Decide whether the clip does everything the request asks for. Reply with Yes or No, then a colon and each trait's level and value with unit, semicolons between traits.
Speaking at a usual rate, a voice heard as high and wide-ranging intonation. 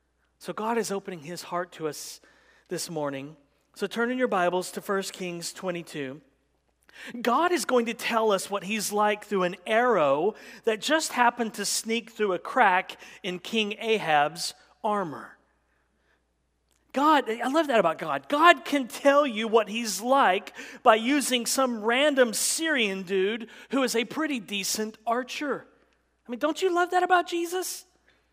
Yes: average, 160 wpm; high, 225 Hz; wide, 5.9 semitones